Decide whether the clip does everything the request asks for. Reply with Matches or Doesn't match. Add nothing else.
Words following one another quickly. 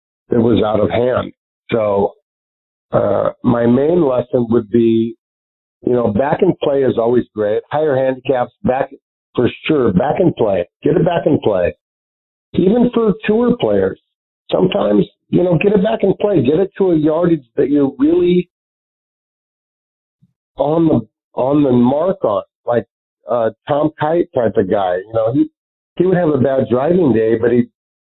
Doesn't match